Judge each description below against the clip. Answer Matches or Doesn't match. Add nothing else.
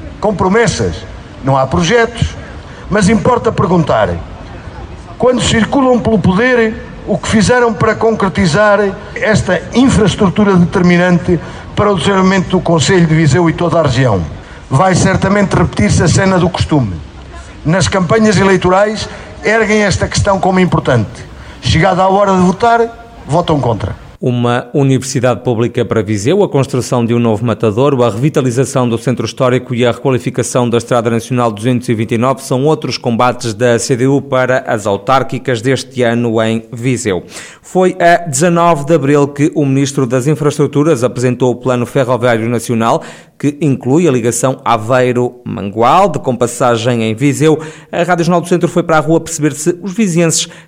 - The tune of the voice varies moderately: Doesn't match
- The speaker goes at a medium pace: Matches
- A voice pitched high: Doesn't match